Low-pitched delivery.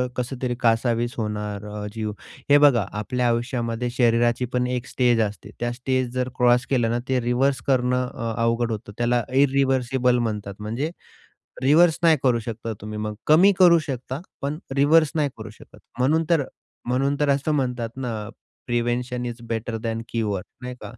Yes: low, 125 Hz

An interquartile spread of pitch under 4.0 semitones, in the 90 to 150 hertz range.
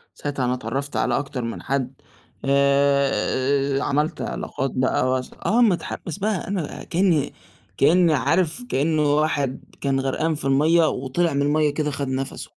Yes: average, 2.8 semitones; medium, 140 Hz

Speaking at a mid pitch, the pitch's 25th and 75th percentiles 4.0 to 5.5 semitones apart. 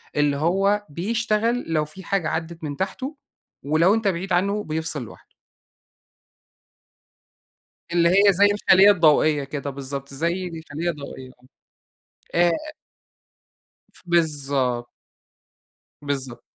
Yes: medium, 165 Hz; average, 5.2 semitones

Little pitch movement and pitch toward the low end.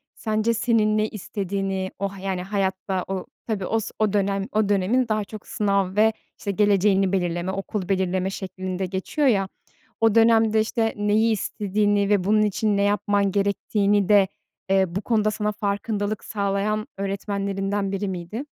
No: narrow, 1.7 semitones; high, 200 Hz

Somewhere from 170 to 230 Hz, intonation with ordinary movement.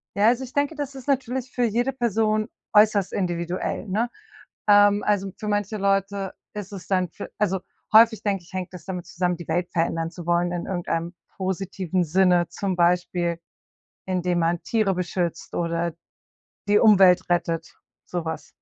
Yes: high, 190 Hz; average, 3.3 semitones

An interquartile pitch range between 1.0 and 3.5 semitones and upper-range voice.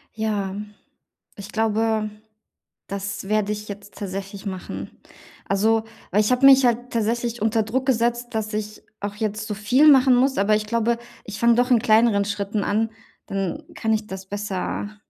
Yes: narrow, 2.4 semitones; high, 215 Hz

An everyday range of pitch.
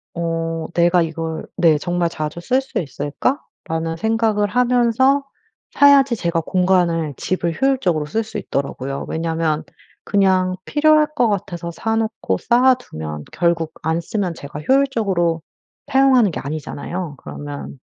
No: wide, 5.9 semitones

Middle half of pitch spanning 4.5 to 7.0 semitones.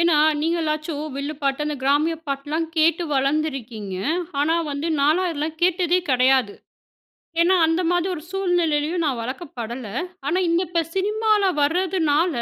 No: average, 3.7 semitones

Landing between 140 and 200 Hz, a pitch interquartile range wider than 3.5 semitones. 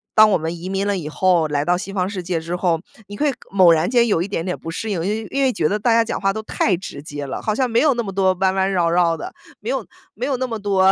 Yes: high, 190 Hz; average, 4.0 semitones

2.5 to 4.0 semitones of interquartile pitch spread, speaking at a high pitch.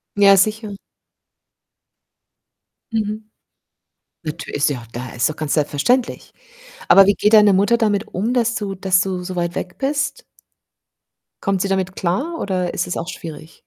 Yes: average, 3.7 semitones; high, 195 Hz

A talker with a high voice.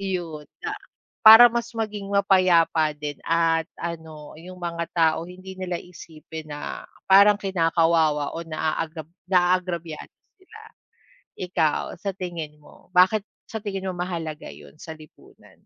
No: medium, 170 Hz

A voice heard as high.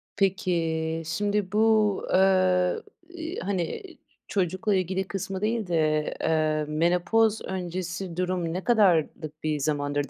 No: medium, 180 Hz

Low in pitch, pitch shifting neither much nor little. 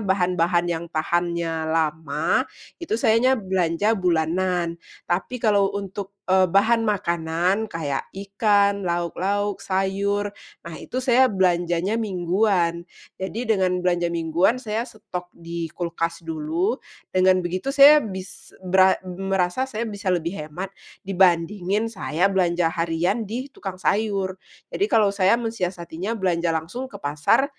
No: medium, 185 Hz; average, 3.2 semitones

